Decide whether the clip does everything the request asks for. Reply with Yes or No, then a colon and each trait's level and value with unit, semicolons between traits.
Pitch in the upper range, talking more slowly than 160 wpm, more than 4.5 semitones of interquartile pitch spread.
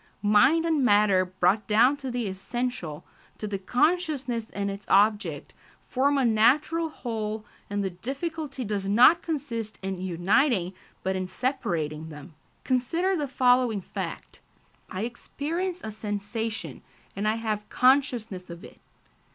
Yes: high, 225 Hz; slow, 135 wpm; wide, 5.5 semitones